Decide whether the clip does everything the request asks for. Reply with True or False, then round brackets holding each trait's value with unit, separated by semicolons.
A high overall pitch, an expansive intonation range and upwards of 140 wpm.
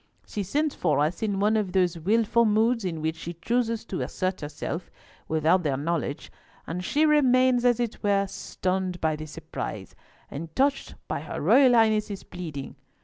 True (195 Hz; 5.8 semitones; 170 wpm)